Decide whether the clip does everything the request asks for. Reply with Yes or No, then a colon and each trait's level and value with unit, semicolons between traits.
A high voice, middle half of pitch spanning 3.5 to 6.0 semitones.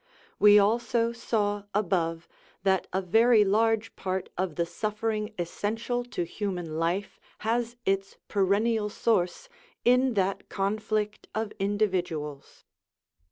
No: high, 205 Hz; average, 3.1 semitones